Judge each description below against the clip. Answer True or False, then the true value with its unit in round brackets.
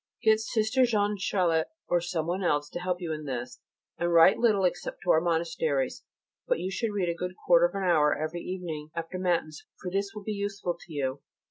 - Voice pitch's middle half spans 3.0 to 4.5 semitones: True (3.5 semitones)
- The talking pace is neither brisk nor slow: False (210 wpm)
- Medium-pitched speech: True (175 Hz)